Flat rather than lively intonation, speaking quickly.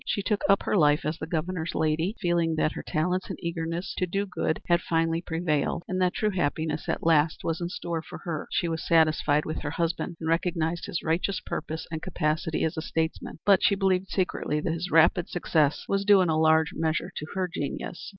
Yes: narrow, 2.3 semitones; fast, 215 wpm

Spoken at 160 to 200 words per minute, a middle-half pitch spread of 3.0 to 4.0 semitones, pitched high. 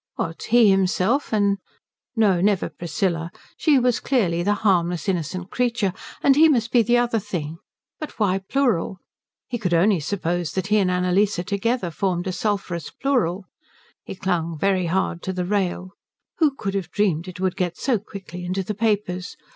Yes: average, 170 wpm; average, 3.4 semitones; high, 195 Hz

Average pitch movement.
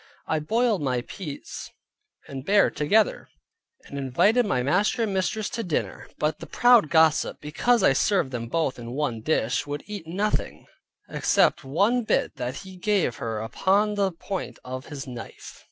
No: wide, 7.5 semitones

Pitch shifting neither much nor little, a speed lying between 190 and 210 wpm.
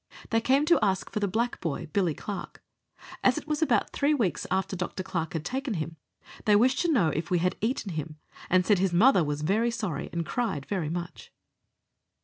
No: wide, 5.9 semitones; fast, 205 wpm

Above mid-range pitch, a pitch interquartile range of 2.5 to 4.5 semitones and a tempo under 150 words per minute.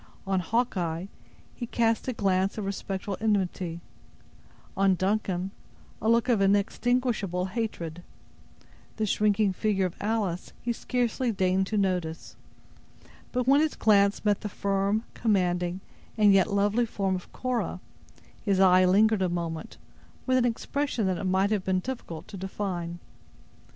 Yes: high, 200 Hz; average, 3.1 semitones; average, 140 wpm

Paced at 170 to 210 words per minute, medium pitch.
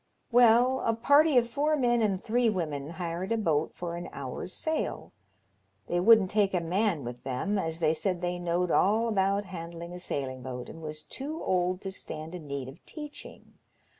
Yes: average, 190 wpm; medium, 180 Hz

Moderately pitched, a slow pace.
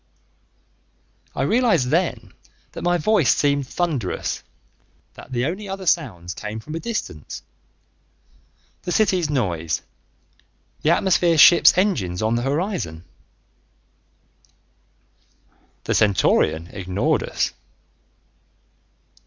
Yes: medium, 145 Hz; slow, 95 wpm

